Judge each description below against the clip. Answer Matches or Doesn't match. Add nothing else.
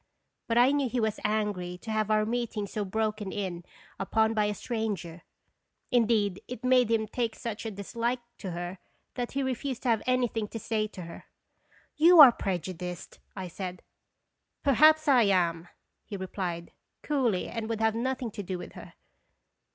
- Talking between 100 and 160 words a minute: Doesn't match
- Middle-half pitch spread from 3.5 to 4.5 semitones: Matches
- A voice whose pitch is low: Doesn't match